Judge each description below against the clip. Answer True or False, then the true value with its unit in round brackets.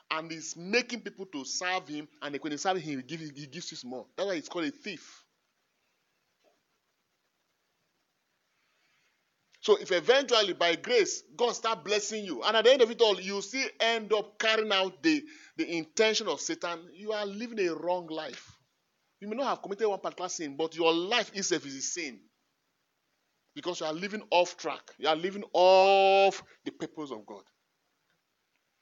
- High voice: True (195 Hz)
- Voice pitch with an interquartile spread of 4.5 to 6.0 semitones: True (5.1 semitones)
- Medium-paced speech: True (180 wpm)